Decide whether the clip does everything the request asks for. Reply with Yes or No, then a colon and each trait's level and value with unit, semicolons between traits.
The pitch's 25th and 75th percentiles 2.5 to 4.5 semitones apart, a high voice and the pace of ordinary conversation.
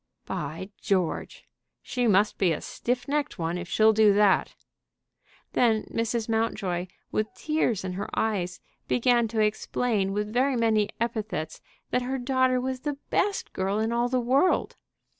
Yes: average, 4.0 semitones; high, 220 Hz; average, 155 wpm